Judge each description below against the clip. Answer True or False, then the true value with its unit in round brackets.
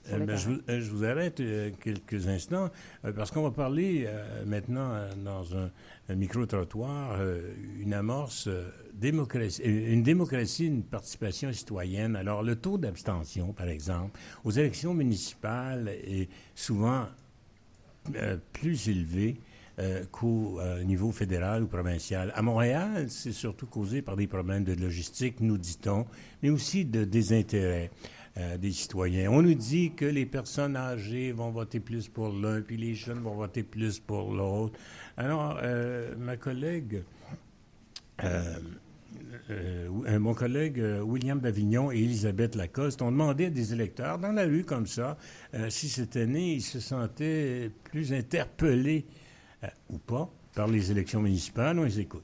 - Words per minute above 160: False (155 wpm)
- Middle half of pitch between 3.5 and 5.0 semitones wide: True (4.5 semitones)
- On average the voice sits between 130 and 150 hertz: False (115 Hz)